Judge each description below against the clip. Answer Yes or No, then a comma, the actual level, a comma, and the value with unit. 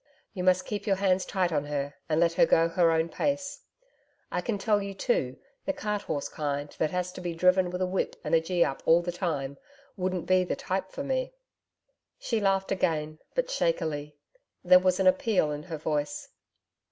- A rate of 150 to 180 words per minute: No, average, 200 wpm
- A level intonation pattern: No, average, 3.6 semitones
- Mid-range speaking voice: Yes, medium, 180 Hz